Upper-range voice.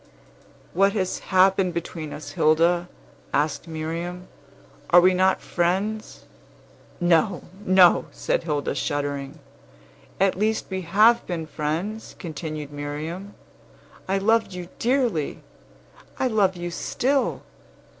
No: medium, 175 Hz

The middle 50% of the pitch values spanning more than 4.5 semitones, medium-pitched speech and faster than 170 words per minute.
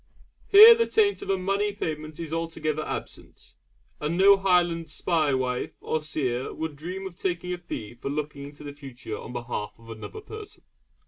Yes: average, 5.0 semitones; medium, 160 Hz; average, 180 wpm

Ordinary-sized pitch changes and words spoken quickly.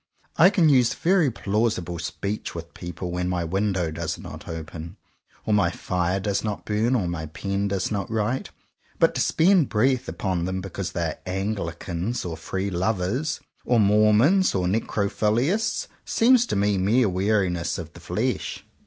No: average, 4.5 semitones; average, 160 wpm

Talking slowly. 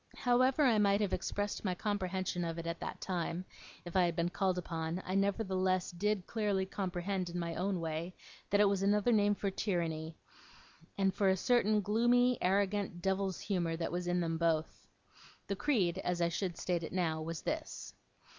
No: average, 185 wpm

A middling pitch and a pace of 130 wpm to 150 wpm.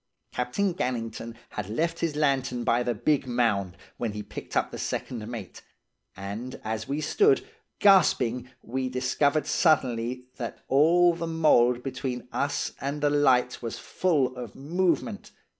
No: low, 130 Hz; average, 145 wpm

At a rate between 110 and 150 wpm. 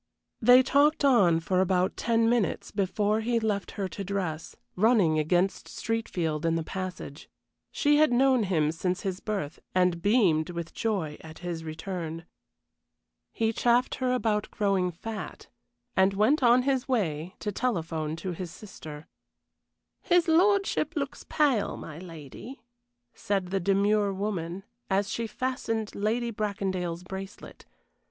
Yes: average, 140 wpm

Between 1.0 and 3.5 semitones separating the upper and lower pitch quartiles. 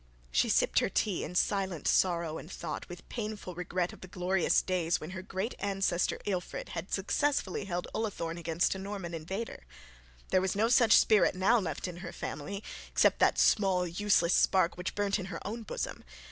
Yes: narrow, 2.5 semitones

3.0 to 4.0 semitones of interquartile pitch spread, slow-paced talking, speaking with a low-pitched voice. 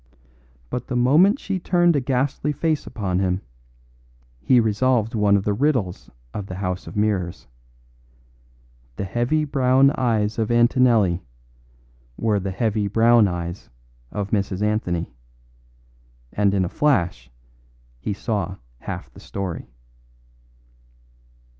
No: average, 4.9 semitones; slow, 120 wpm; low, 105 Hz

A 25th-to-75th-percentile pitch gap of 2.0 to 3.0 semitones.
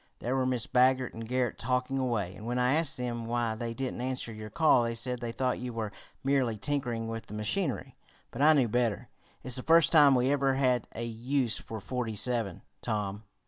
Yes: narrow, 2.5 semitones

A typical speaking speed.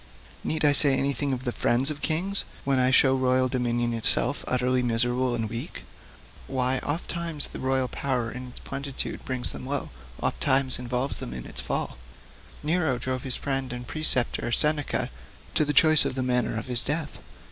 Yes: average, 180 wpm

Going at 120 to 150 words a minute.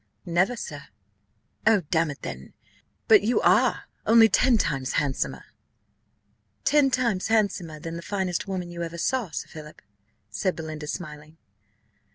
Yes: average, 140 wpm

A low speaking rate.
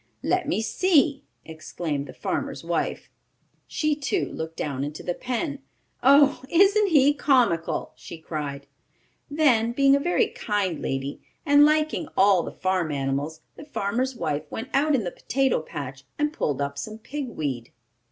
No: average, 155 wpm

